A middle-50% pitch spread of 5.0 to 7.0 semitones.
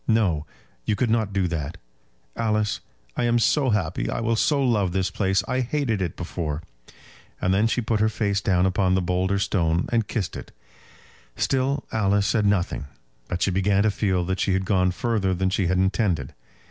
No: average, 3.2 semitones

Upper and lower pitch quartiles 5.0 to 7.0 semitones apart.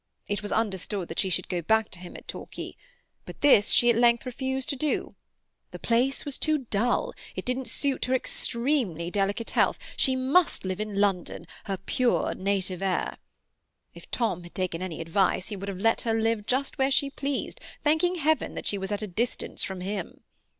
Yes: wide, 5.4 semitones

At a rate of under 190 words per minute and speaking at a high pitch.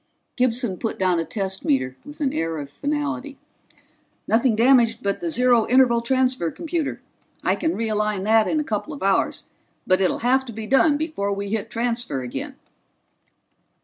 Yes: average, 170 wpm; high, 230 Hz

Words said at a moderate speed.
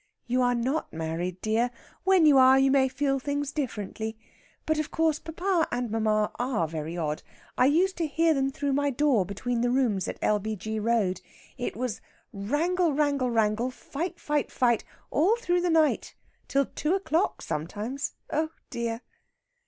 Yes: average, 165 wpm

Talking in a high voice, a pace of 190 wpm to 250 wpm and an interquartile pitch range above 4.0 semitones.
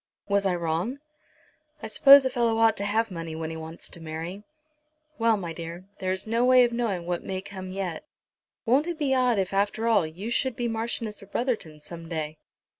Yes: high, 200 Hz; average, 195 wpm; average, 5.3 semitones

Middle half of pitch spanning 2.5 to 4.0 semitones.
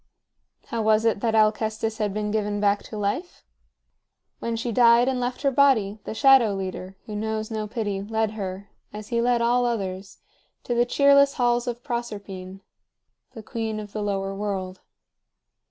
Yes: average, 2.8 semitones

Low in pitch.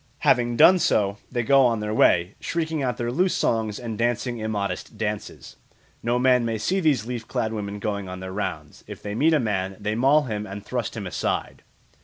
Yes: low, 115 Hz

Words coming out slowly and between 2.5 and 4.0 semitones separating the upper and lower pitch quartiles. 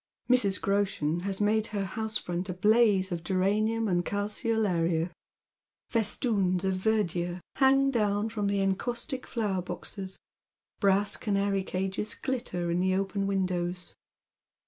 Yes: slow, 125 wpm; average, 2.8 semitones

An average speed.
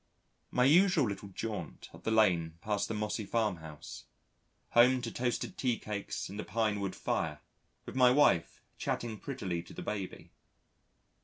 Yes: average, 155 wpm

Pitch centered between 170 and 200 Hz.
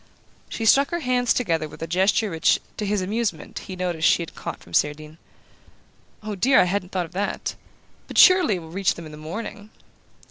Yes: medium, 185 Hz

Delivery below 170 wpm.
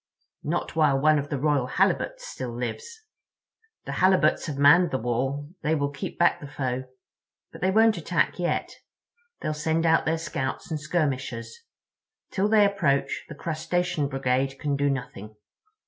Yes: average, 160 wpm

